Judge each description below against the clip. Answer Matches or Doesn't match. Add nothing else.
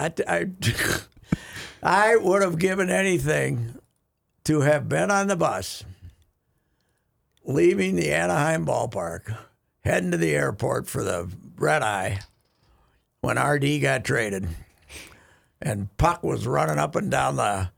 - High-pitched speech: Doesn't match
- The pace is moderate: Doesn't match